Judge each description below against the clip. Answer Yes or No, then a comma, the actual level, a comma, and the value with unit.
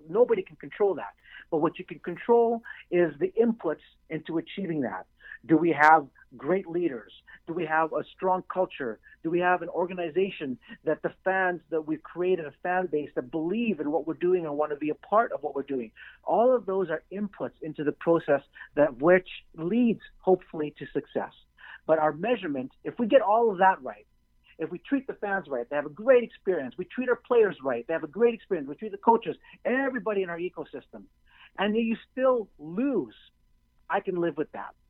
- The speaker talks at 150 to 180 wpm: No, fast, 205 wpm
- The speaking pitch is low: No, medium, 175 Hz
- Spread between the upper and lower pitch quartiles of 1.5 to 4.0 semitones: No, wide, 5.4 semitones